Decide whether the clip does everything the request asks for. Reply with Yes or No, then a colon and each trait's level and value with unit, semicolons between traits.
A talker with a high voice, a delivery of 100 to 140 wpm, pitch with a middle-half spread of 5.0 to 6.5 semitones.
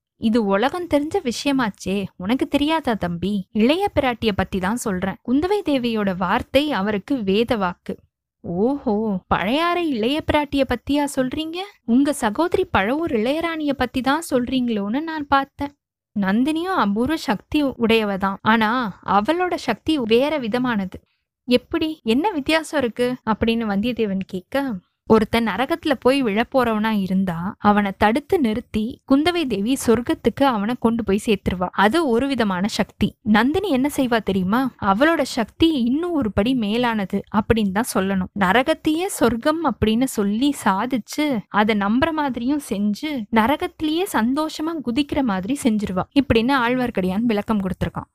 Yes: high, 240 Hz; average, 125 wpm; average, 5.3 semitones